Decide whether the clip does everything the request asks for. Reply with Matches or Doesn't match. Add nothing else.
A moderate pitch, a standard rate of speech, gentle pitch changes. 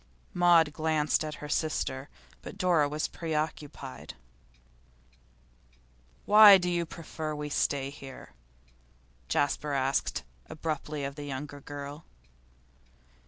Doesn't match